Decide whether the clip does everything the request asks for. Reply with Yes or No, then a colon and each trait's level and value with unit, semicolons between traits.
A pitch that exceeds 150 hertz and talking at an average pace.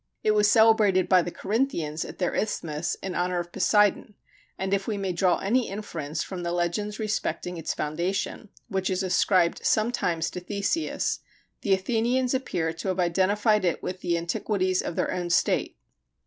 Yes: high, 190 Hz; average, 170 wpm